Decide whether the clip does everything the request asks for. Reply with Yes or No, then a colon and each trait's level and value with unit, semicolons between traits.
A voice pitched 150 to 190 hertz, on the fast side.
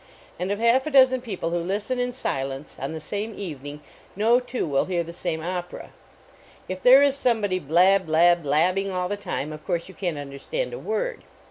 Yes: medium, 185 Hz; fast, 210 wpm